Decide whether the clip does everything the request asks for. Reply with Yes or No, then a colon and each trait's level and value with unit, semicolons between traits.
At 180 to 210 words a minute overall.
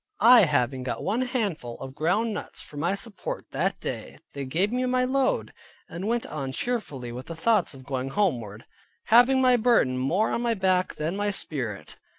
Yes: average, 190 wpm